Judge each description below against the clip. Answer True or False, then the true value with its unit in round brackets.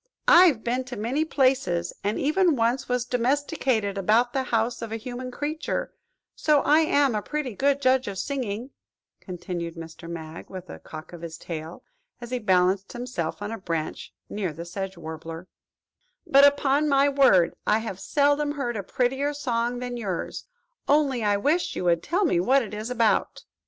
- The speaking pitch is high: True (240 Hz)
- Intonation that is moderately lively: False (6.6 semitones)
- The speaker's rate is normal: True (180 wpm)